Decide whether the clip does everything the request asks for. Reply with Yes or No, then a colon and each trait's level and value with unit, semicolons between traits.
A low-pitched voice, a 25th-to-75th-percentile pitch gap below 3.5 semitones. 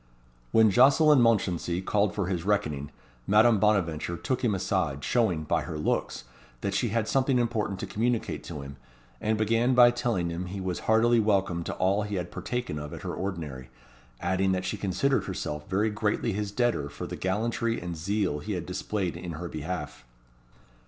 No: low, 100 Hz; average, 4.5 semitones